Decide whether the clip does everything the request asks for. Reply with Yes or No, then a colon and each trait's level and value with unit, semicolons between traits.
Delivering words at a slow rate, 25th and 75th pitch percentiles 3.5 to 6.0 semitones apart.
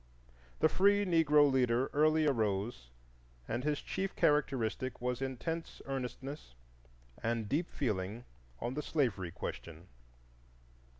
Yes: slow, 110 wpm; average, 4.7 semitones